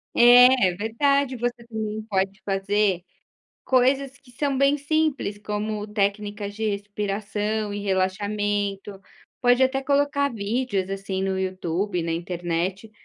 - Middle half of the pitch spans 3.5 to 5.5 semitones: Yes, average, 4.0 semitones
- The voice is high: Yes, high, 210 Hz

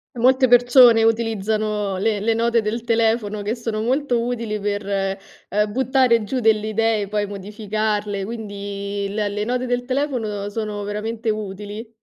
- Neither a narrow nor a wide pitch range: No, narrow, 2.2 semitones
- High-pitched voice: Yes, high, 215 Hz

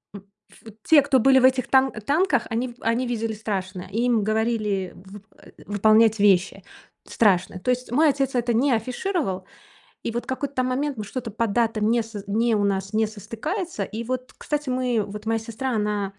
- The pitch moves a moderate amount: Yes, average, 3.5 semitones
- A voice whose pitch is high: Yes, high, 230 Hz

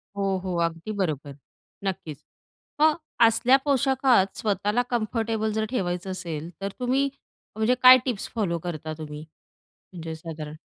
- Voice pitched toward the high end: Yes, high, 195 Hz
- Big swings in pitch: Yes, wide, 6.4 semitones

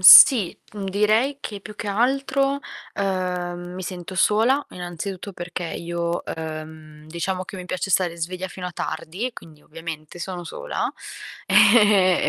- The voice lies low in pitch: No, medium, 185 Hz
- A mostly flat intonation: No, average, 3.2 semitones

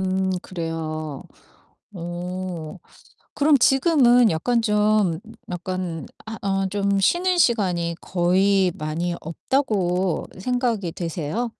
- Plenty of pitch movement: No, average, 4.5 semitones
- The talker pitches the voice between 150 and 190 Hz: Yes, medium, 185 Hz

